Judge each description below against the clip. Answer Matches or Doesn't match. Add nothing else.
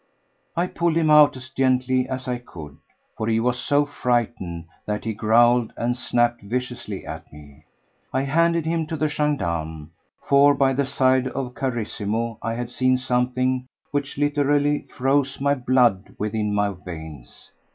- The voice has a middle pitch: Doesn't match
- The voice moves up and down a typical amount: Matches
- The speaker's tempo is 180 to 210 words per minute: Doesn't match